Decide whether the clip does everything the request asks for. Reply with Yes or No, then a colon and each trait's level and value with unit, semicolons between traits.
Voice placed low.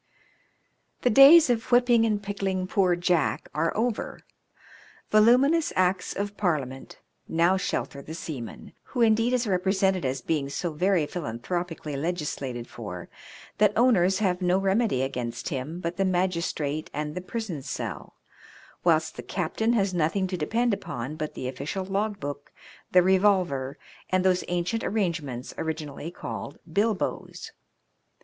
No: medium, 180 Hz